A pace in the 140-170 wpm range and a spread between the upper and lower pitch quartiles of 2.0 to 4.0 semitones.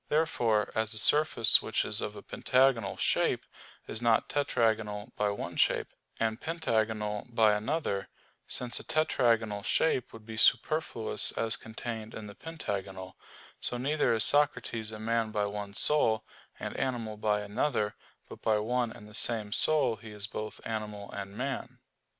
Yes: average, 155 wpm; average, 2.8 semitones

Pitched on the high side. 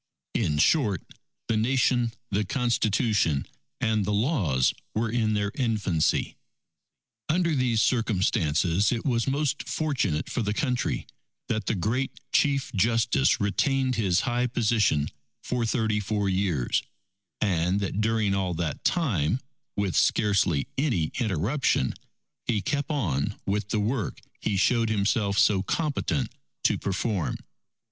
No: low, 110 Hz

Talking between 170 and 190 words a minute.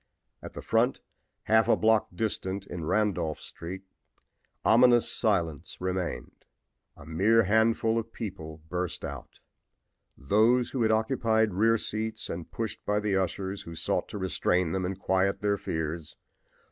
No: average, 145 wpm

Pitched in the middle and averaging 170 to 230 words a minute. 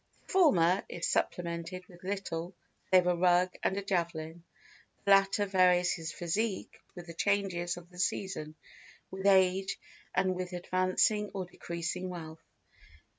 No: medium, 180 Hz; average, 140 wpm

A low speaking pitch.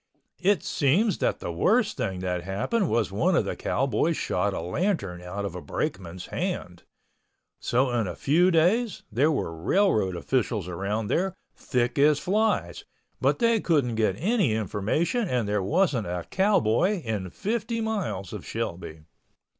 Yes: low, 125 Hz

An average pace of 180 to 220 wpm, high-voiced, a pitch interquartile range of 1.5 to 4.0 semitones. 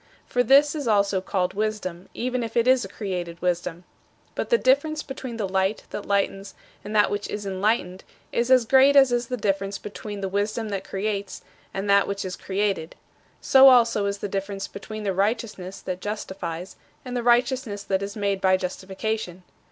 Yes: average, 185 wpm; high, 205 Hz; average, 3.5 semitones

